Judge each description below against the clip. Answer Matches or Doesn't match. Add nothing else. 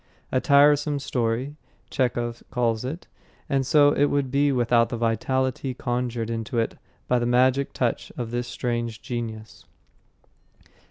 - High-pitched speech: Doesn't match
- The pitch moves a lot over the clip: Doesn't match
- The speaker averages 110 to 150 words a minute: Matches